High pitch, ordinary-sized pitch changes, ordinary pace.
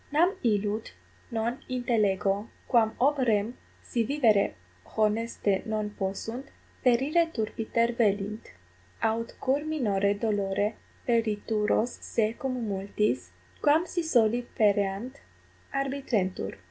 No: high, 225 Hz; average, 3.5 semitones; slow, 100 wpm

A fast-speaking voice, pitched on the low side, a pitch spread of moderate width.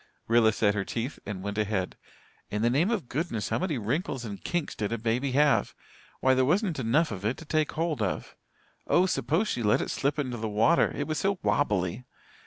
No: fast, 210 wpm; low, 125 Hz; wide, 6.4 semitones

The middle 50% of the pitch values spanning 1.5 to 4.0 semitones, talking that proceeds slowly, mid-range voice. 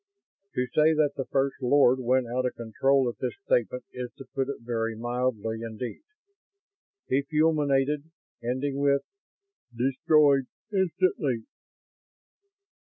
No: average, 2.7 semitones; slow, 125 wpm; low, 130 Hz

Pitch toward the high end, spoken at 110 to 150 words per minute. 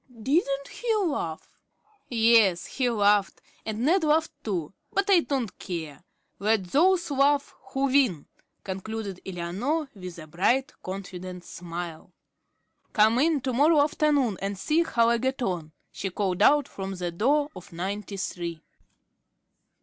Yes: high, 220 Hz; average, 140 wpm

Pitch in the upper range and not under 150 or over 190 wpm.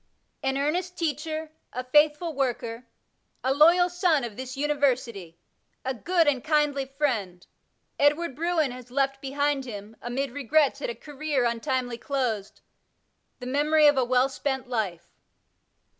No: very high, 275 Hz; average, 140 wpm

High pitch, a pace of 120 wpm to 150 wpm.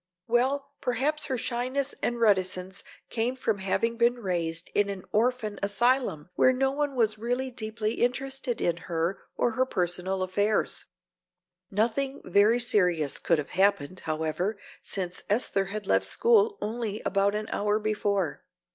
Yes: high, 215 Hz; average, 145 wpm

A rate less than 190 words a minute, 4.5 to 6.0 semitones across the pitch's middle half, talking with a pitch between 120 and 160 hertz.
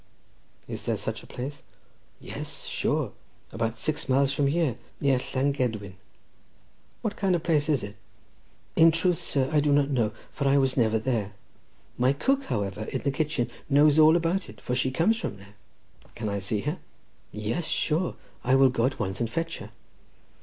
Yes: average, 180 wpm; average, 5.1 semitones; low, 135 Hz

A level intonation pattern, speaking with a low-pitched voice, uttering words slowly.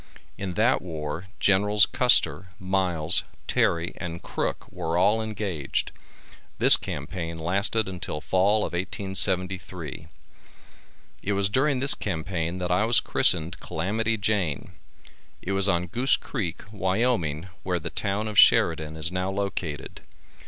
No: average, 3.7 semitones; very low, 95 Hz; slow, 130 wpm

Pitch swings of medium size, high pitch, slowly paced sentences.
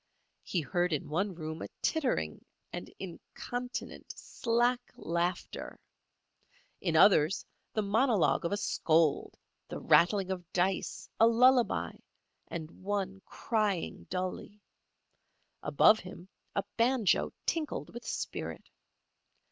Yes: average, 5.0 semitones; high, 195 Hz; slow, 110 wpm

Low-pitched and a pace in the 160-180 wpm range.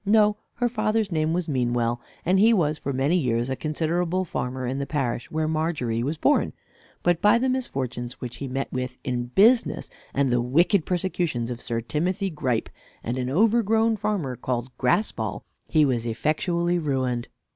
No: medium, 150 Hz; average, 170 wpm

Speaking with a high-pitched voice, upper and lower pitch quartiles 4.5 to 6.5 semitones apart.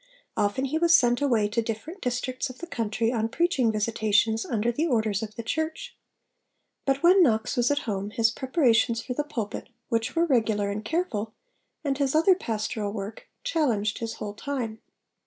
Yes: high, 235 Hz; average, 4.8 semitones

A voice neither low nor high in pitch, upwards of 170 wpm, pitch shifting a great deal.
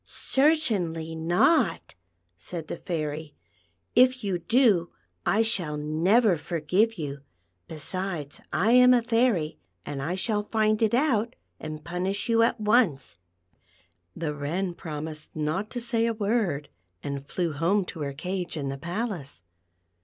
No: medium, 180 Hz; average, 140 wpm; wide, 6.6 semitones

